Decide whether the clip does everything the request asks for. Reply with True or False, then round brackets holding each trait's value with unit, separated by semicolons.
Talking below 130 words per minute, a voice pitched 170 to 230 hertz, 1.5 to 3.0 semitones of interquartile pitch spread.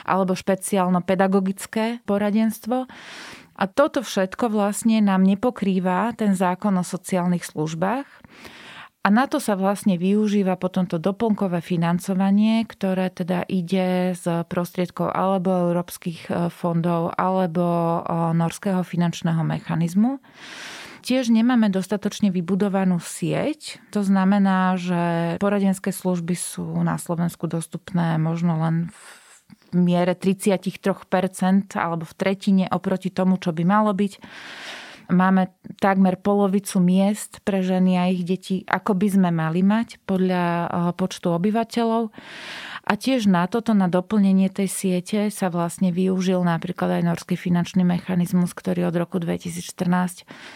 True (120 wpm; 185 Hz; 2.4 semitones)